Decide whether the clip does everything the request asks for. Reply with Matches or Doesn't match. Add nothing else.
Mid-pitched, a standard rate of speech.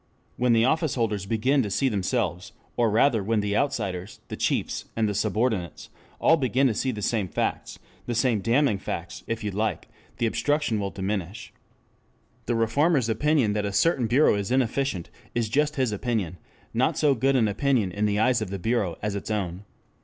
Doesn't match